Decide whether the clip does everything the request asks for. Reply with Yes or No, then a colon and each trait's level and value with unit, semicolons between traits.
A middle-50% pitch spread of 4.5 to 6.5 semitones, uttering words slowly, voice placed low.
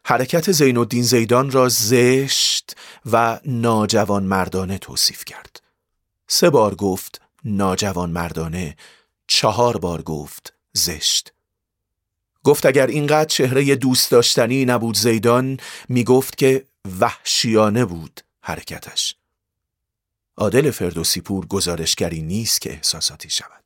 Yes: average, 5.1 semitones; slow, 100 wpm; low, 115 Hz